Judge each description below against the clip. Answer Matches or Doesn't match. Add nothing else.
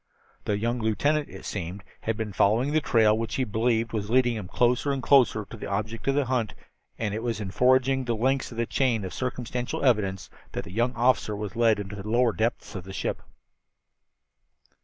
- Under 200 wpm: Doesn't match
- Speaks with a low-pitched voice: Matches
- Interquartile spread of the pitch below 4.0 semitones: Matches